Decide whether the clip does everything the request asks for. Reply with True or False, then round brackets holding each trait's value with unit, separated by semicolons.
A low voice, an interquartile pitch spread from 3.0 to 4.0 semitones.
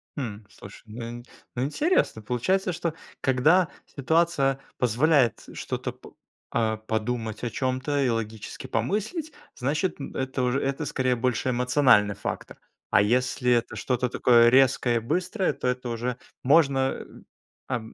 True (125 Hz; 3.5 semitones)